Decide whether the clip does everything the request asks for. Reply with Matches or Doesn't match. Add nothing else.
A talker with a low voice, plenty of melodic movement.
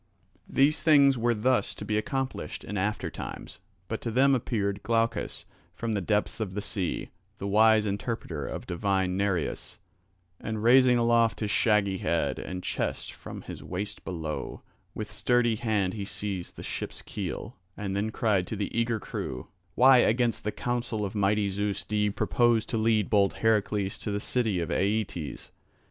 Doesn't match